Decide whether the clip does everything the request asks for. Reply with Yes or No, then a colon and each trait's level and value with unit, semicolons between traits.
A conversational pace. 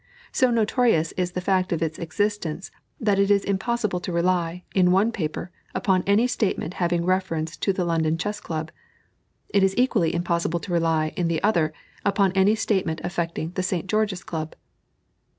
Yes: average, 170 wpm